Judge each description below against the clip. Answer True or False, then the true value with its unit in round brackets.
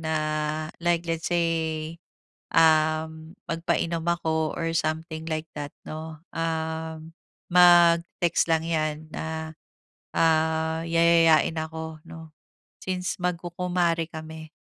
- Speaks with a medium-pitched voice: True (160 Hz)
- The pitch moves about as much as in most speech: False (1.0 semitones)